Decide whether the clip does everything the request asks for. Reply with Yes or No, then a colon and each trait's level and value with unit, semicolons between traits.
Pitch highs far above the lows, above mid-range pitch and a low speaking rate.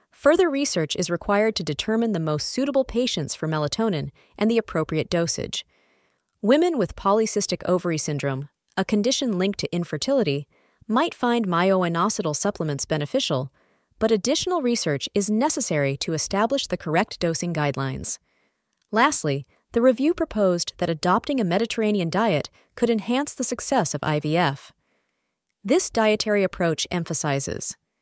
Yes: wide, 6.9 semitones; high, 195 Hz; slow, 130 wpm